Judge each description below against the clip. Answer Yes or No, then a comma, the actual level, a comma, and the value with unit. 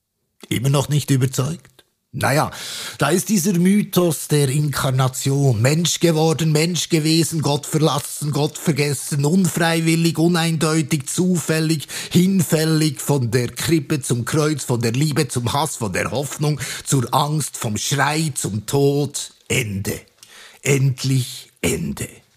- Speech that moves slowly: Yes, slow, 120 wpm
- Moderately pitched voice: Yes, medium, 150 Hz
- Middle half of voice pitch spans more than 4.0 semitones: No, average, 3.3 semitones